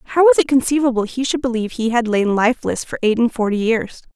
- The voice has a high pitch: Yes, high, 235 Hz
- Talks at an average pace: No, fast, 230 wpm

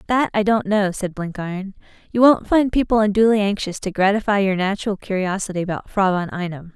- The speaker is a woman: Yes, female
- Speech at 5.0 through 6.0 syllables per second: Yes, 5.8 syllables/s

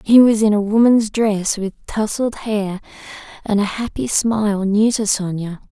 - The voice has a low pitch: No, high, 210 Hz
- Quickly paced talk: No, average, 170 wpm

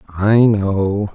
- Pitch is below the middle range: Yes, low, 100 Hz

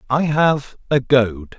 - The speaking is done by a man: Yes, male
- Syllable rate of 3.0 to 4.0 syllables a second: Yes, 3.2 syllables/s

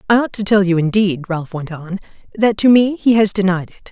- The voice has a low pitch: No, high, 195 Hz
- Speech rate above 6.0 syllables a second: No, 5.6 syllables/s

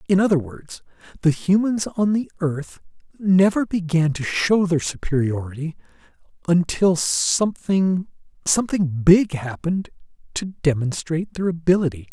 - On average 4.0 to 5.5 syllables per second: Yes, 4.6 syllables/s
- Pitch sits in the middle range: Yes, medium, 170 Hz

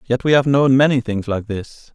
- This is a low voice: Yes, low, 125 Hz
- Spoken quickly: Yes, fast, 245 wpm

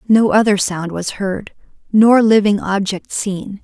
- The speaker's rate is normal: Yes, average, 150 wpm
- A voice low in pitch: No, high, 205 Hz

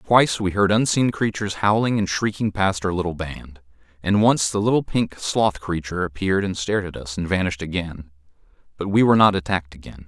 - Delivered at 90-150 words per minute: No, average, 195 wpm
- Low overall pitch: Yes, very low, 95 Hz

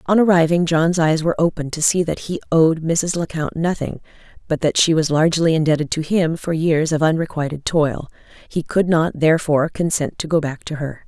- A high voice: No, medium, 160 Hz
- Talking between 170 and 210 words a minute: Yes, fast, 205 wpm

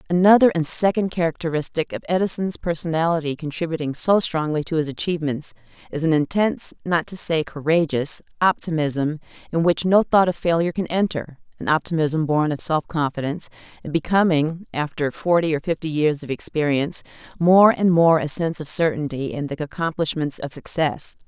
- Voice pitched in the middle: Yes, medium, 160 Hz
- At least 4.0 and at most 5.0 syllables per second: No, 5.5 syllables/s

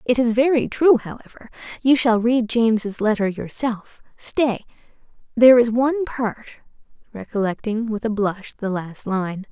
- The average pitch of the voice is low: No, high, 225 Hz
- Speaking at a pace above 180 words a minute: No, average, 140 wpm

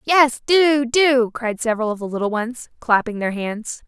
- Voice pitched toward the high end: Yes, high, 240 Hz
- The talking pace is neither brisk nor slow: Yes, average, 185 wpm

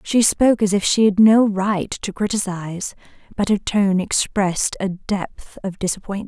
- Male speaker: No, female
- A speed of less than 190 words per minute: Yes, average, 170 wpm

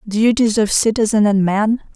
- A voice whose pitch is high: Yes, high, 215 Hz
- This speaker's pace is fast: No, average, 155 wpm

